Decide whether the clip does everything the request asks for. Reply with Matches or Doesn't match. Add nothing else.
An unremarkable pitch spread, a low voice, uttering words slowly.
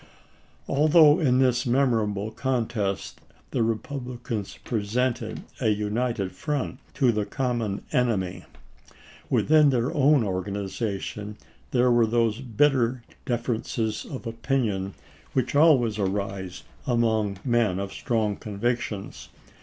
Matches